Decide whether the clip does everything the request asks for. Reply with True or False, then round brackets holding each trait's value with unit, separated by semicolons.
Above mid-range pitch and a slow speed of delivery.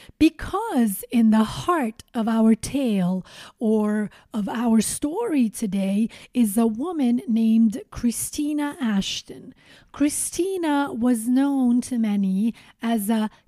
True (230 Hz; 110 wpm)